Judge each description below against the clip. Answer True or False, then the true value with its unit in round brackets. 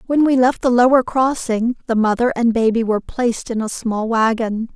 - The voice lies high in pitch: True (235 Hz)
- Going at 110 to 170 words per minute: False (200 wpm)